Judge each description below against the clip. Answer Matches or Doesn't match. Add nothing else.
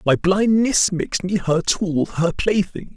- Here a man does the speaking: Matches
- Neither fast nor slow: Matches